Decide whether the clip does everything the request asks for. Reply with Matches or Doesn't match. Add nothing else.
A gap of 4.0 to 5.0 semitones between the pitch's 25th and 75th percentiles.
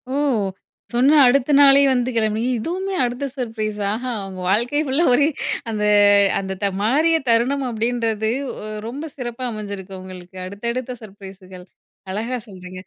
Matches